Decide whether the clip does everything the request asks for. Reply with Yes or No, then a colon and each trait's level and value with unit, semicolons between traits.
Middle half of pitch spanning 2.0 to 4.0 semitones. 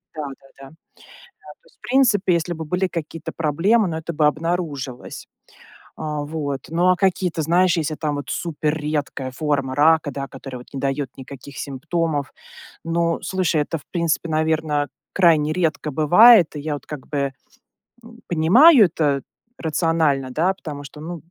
Yes: average, 2.9 semitones